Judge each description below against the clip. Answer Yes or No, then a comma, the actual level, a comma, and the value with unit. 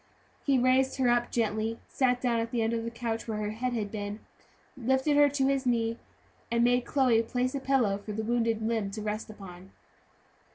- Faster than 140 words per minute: Yes, fast, 205 wpm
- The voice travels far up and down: No, average, 2.7 semitones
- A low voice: No, high, 235 Hz